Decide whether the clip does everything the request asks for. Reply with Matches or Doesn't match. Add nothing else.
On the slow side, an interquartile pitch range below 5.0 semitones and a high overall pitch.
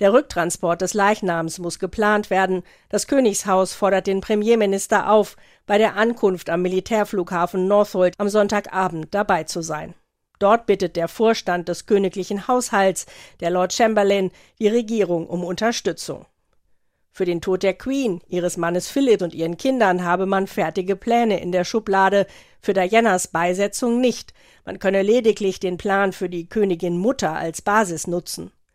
Doesn't match